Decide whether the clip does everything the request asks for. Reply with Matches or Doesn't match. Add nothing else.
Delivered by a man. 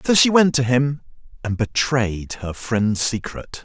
Matches